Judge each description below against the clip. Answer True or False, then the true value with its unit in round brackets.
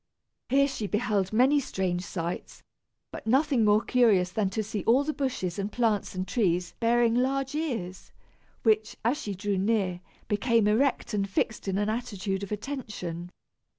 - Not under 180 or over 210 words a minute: False (160 wpm)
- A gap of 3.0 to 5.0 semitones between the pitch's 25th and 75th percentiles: True (4.3 semitones)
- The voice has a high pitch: True (215 Hz)